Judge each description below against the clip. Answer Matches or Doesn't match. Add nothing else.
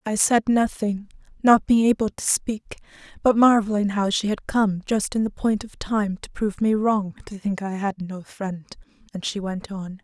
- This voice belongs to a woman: Matches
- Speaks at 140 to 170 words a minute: Doesn't match